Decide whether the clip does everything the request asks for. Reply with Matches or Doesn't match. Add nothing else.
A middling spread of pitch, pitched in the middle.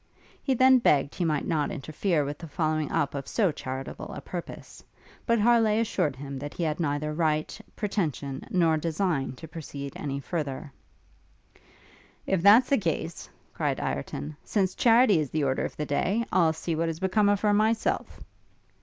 Doesn't match